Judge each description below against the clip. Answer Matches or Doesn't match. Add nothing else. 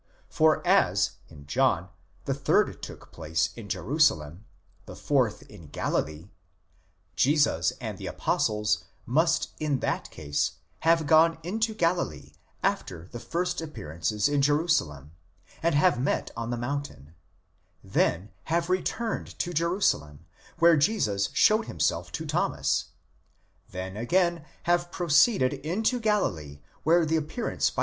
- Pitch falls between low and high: Matches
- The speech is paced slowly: Matches